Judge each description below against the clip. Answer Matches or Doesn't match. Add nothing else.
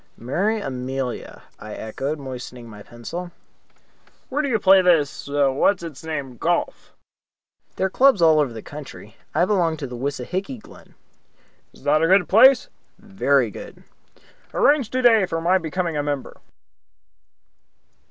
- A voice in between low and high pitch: Matches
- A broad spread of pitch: Matches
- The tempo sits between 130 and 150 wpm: Matches